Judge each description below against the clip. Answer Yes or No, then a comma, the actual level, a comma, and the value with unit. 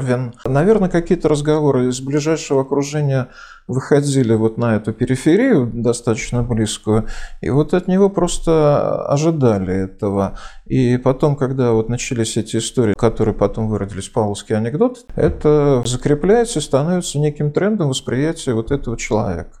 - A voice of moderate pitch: No, low, 130 Hz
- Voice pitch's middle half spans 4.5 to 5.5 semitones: Yes, average, 5.0 semitones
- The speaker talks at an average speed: Yes, average, 130 wpm